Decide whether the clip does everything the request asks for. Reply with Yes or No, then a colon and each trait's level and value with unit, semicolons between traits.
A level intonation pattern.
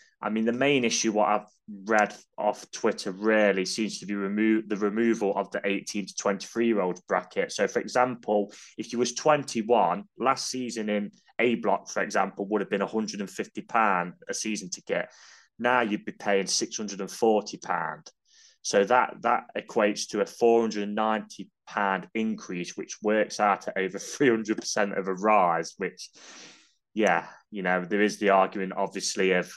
Yes: narrow, 2.0 semitones